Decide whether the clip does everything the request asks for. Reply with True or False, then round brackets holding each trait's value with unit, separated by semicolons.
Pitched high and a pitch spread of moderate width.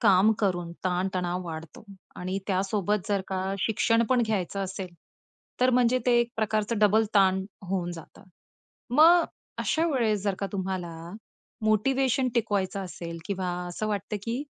True (200 Hz; 3.7 semitones)